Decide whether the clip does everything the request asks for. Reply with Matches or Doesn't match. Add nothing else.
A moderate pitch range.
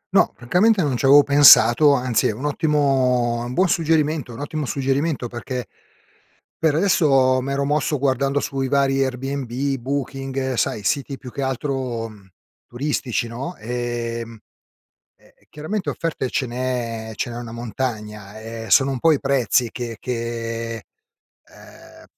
Matches